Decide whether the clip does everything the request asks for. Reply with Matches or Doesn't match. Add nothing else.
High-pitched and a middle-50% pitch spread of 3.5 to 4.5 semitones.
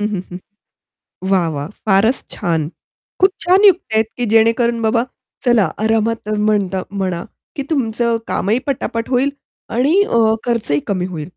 Matches